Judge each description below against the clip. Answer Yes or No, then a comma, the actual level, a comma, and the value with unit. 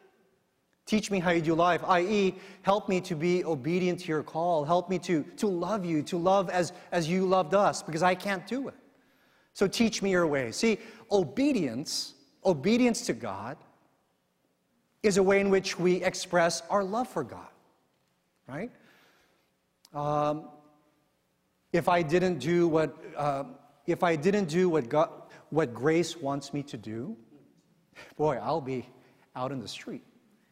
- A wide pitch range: No, average, 4.5 semitones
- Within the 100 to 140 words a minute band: No, average, 160 wpm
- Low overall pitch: No, medium, 175 Hz